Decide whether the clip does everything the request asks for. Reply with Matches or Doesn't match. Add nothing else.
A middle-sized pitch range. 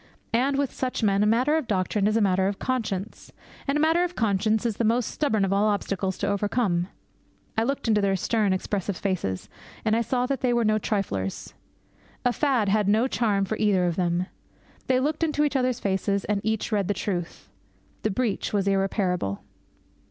Matches